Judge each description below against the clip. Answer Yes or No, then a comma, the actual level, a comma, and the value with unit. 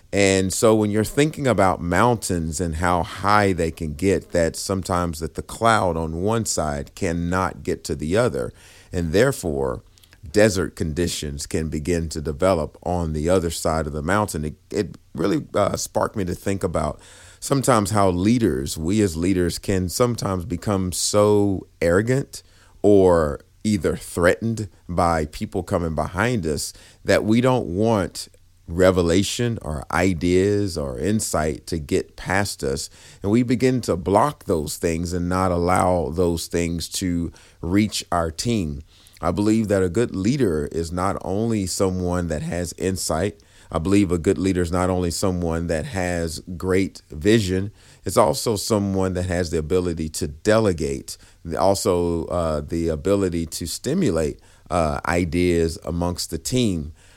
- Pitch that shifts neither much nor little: Yes, average, 3.2 semitones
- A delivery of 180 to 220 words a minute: No, average, 150 wpm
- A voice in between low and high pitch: No, very low, 90 Hz